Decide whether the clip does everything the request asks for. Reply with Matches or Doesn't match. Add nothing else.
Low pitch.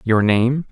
Matches